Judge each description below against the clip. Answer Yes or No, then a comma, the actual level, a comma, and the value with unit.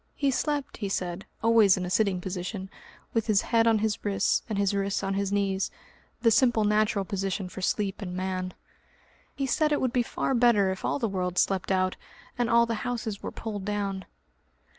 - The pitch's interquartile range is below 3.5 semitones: Yes, average, 3.1 semitones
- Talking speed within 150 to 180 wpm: No, average, 200 wpm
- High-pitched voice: Yes, high, 200 Hz